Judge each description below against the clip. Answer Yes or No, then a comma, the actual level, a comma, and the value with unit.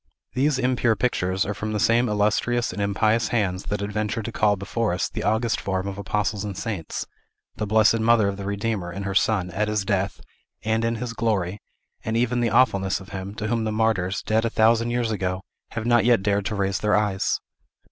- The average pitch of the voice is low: Yes, low, 105 Hz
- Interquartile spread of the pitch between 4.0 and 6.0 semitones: No, narrow, 2.6 semitones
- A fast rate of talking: Yes, fast, 210 wpm